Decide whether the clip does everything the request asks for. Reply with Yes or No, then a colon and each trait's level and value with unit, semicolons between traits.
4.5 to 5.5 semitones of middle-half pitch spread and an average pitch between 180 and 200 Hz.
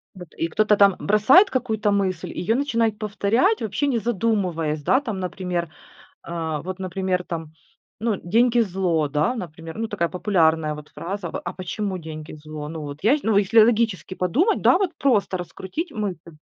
Yes: average, 4.9 semitones; high, 190 Hz